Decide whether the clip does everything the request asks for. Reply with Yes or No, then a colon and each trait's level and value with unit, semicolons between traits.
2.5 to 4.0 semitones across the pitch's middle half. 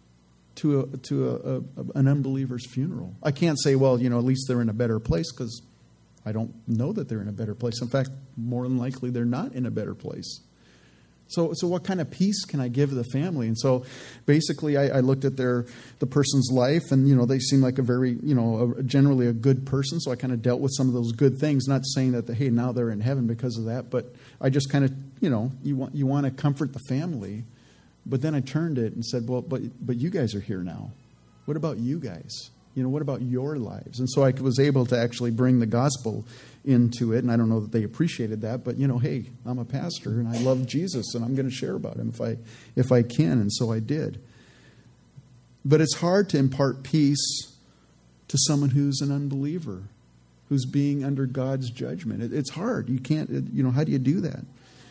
Yes: average, 2.8 semitones